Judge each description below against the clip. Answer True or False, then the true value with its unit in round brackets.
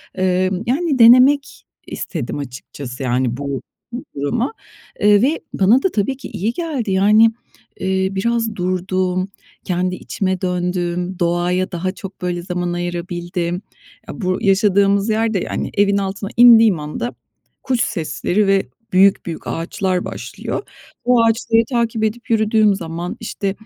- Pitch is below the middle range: False (190 Hz)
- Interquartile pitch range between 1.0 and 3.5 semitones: False (4.0 semitones)